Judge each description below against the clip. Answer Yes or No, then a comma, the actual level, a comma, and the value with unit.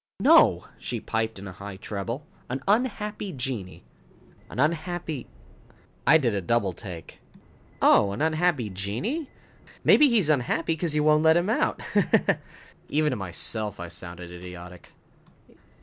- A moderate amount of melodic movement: No, wide, 8.7 semitones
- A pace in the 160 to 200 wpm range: No, average, 150 wpm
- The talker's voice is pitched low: Yes, low, 125 Hz